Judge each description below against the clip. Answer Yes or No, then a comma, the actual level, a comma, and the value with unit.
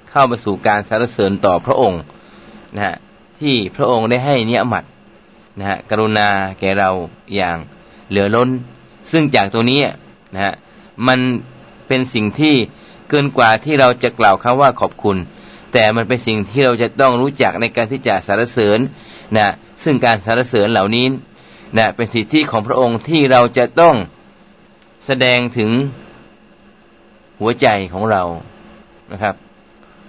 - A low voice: Yes, low, 115 Hz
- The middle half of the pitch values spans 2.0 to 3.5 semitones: No, average, 3.9 semitones